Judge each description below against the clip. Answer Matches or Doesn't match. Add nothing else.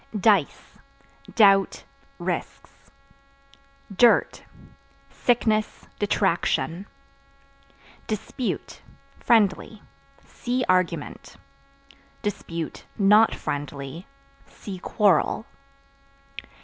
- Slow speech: Matches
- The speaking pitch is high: Matches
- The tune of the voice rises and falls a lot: Doesn't match